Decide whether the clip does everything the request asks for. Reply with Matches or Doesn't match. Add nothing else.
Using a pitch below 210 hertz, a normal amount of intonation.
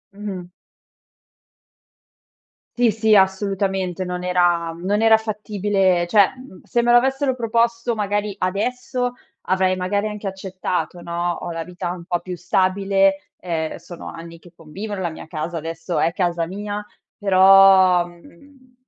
Matches